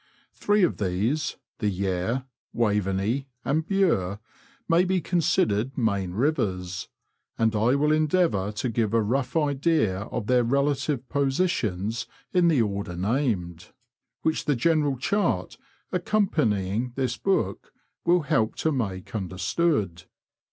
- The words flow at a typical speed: No, slow, 130 wpm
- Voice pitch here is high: No, low, 125 Hz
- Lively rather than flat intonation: Yes, wide, 7.4 semitones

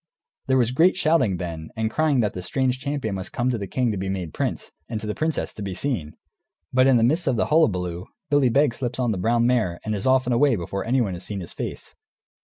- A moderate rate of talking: No, fast, 250 wpm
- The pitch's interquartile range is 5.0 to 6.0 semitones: Yes, average, 5.3 semitones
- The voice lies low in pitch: Yes, low, 115 Hz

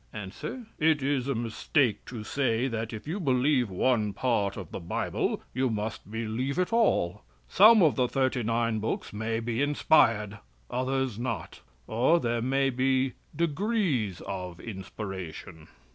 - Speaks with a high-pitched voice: No, low, 120 Hz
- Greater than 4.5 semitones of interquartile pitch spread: No, average, 4.1 semitones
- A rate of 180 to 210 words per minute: No, average, 145 wpm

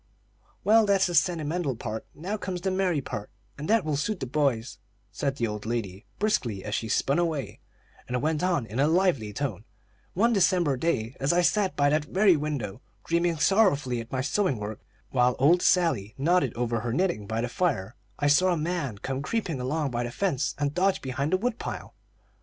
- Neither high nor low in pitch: Yes, medium, 145 Hz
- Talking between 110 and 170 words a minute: No, average, 200 wpm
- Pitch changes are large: Yes, wide, 6.7 semitones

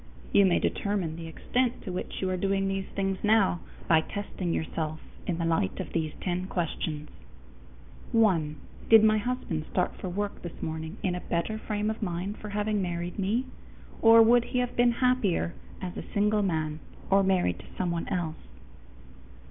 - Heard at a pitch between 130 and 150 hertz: No, high, 190 Hz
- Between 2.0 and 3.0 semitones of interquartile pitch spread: No, average, 3.9 semitones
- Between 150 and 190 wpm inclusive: Yes, average, 175 wpm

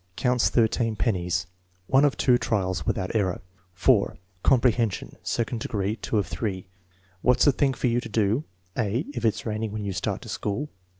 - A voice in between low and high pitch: No, low, 110 Hz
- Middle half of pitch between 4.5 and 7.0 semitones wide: No, average, 3.8 semitones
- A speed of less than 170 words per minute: No, average, 180 wpm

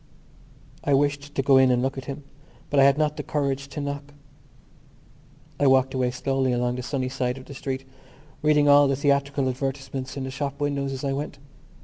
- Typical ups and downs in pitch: No, narrow, 1.3 semitones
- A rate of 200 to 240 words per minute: Yes, fast, 205 wpm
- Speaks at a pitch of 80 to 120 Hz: No, low, 135 Hz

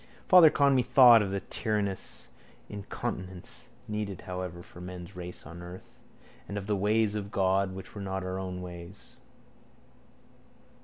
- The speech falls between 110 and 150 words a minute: Yes, average, 140 wpm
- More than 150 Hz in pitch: No, very low, 95 Hz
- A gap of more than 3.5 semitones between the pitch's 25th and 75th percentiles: No, narrow, 2.5 semitones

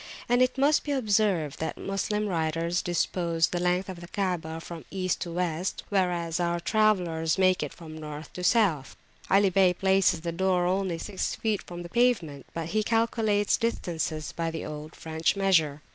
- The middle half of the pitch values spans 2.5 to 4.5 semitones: Yes, average, 3.3 semitones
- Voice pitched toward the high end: No, medium, 180 Hz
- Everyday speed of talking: Yes, average, 175 wpm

